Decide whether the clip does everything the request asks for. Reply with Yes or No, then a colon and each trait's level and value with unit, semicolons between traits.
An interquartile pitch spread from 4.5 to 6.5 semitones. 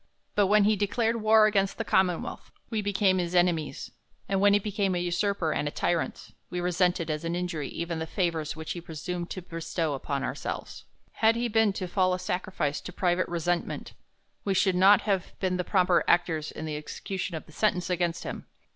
No: average, 2.9 semitones